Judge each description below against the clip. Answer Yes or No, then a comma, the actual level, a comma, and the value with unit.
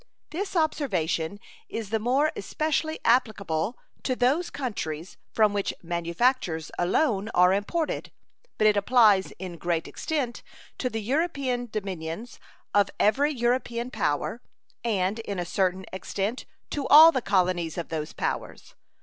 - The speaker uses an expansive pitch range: Yes, wide, 5.8 semitones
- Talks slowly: Yes, slow, 130 wpm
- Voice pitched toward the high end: Yes, high, 215 Hz